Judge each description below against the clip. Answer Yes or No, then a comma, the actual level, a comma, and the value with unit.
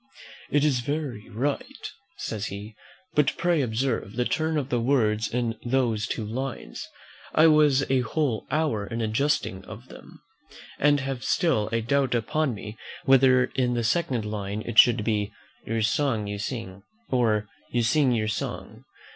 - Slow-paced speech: No, average, 160 wpm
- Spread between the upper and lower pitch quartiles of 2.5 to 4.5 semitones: Yes, average, 4.2 semitones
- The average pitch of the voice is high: No, low, 120 Hz